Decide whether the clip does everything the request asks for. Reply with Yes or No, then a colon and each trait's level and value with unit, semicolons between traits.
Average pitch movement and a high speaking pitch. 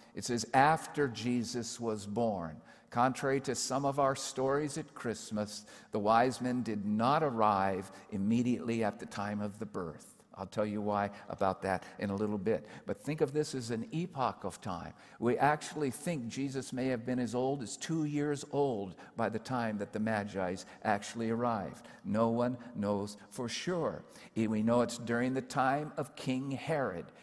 No: average, 4.1 semitones; low, 120 Hz